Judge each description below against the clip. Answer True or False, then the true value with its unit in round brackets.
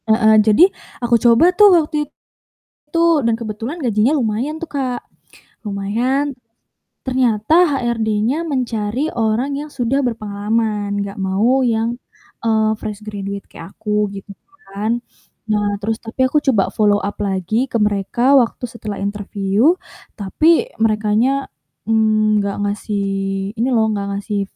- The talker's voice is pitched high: True (220 Hz)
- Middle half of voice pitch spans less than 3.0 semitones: False (3.6 semitones)